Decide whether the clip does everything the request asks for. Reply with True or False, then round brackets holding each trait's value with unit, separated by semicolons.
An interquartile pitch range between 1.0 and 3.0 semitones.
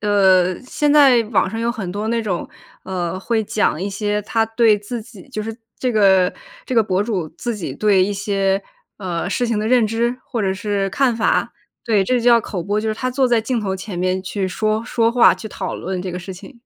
False (3.4 semitones)